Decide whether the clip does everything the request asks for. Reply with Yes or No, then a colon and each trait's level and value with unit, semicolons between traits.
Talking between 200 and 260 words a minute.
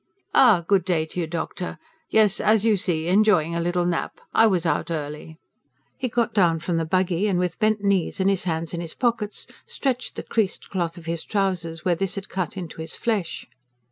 Yes: fast, 205 wpm